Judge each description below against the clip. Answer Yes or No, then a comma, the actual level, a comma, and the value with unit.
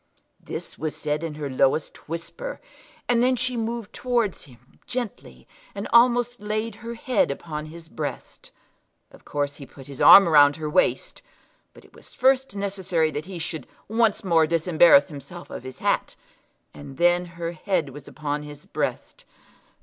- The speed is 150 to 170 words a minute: Yes, average, 165 wpm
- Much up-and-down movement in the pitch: Yes, wide, 7.1 semitones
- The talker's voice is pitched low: No, medium, 170 Hz